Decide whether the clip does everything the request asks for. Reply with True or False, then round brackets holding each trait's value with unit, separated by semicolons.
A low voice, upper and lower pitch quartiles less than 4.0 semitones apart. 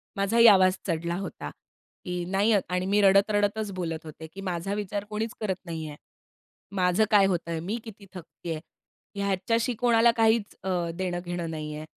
False (190 Hz; 3.2 semitones)